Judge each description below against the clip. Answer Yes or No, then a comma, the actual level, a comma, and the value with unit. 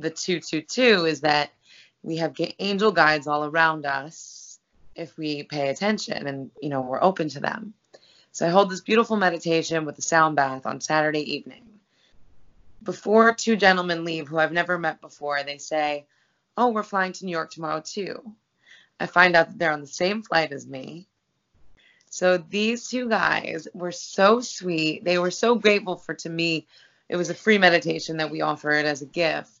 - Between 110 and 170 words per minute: No, average, 185 wpm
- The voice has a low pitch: No, medium, 165 Hz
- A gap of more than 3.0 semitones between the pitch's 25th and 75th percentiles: Yes, average, 4.1 semitones